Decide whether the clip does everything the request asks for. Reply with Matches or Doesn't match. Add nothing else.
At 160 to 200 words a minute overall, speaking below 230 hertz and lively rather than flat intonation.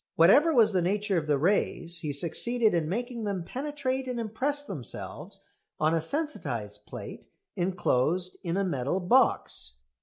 Doesn't match